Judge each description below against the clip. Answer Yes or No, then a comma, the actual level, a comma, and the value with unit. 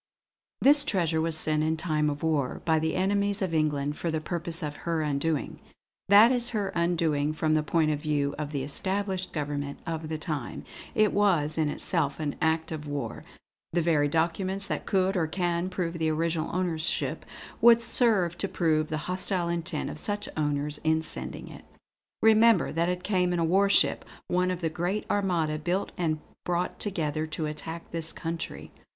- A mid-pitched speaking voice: Yes, medium, 165 Hz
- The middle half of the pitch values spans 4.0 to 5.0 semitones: No, average, 3.1 semitones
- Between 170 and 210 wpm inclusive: Yes, average, 180 wpm